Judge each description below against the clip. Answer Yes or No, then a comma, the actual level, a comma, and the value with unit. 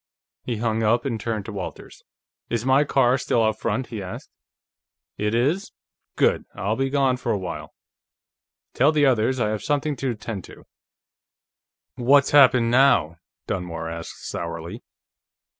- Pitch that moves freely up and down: No, average, 4.4 semitones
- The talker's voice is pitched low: Yes, low, 115 Hz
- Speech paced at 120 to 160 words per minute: Yes, average, 150 wpm